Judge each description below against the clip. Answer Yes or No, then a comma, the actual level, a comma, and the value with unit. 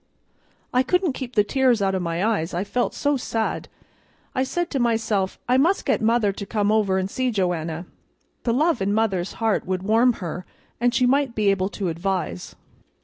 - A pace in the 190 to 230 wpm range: Yes, average, 195 wpm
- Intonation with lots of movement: No, average, 4.8 semitones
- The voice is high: Yes, high, 215 Hz